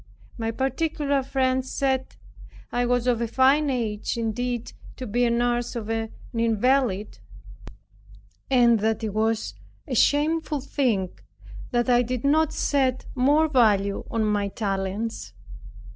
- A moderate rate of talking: No, slow, 130 wpm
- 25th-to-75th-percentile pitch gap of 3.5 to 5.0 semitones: No, average, 3.1 semitones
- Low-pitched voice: No, high, 245 Hz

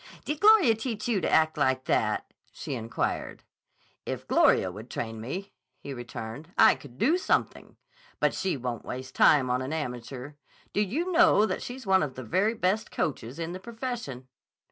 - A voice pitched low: No, medium, 160 Hz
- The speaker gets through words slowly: No, average, 175 wpm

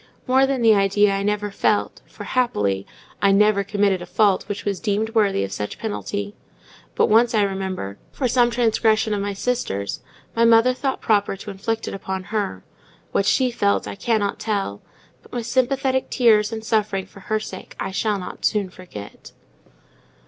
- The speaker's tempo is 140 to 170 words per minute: No, average, 180 wpm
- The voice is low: No, high, 210 Hz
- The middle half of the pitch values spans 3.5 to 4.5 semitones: No, average, 2.7 semitones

